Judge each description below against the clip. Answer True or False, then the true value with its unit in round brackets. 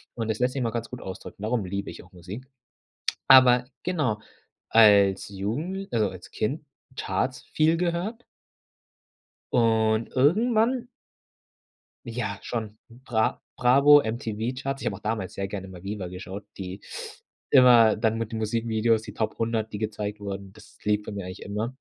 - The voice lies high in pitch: False (110 Hz)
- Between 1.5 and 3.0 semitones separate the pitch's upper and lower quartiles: False (3.8 semitones)